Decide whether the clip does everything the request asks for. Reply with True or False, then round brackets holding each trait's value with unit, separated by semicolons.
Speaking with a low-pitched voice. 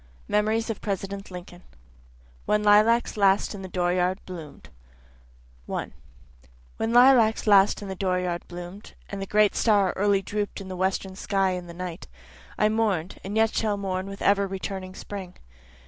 False (195 Hz)